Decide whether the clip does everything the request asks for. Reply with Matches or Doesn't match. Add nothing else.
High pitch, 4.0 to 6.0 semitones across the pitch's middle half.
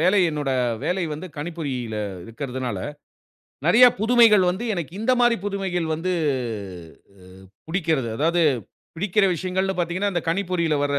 Doesn't match